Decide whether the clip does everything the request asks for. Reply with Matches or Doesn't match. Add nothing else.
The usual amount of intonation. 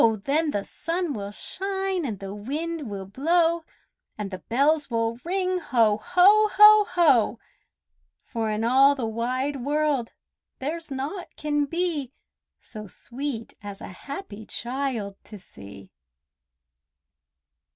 Doesn't match